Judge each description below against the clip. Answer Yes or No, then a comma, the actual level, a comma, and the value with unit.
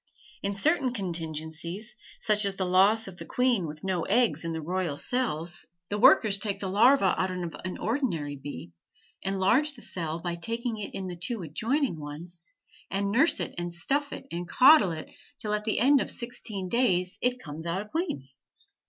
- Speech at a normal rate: Yes, average, 180 wpm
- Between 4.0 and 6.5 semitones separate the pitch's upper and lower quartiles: Yes, wide, 5.6 semitones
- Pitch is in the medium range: No, high, 195 Hz